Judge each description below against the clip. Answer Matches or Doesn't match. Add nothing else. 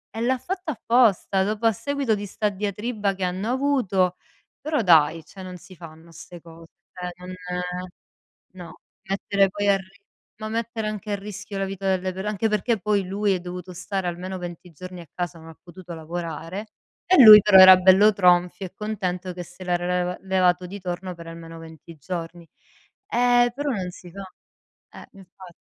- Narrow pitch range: Doesn't match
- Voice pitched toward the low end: Doesn't match